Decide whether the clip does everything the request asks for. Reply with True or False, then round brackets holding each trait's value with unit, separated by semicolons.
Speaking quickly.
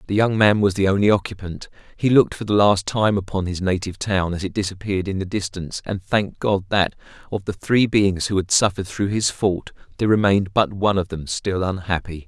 True (220 wpm)